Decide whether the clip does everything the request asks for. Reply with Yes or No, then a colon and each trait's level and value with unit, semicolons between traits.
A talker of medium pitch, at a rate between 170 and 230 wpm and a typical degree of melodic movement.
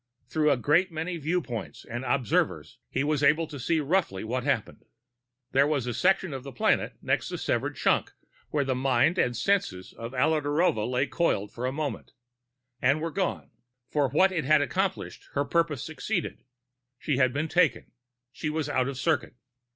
Yes: medium, 145 Hz; average, 180 wpm; average, 4.0 semitones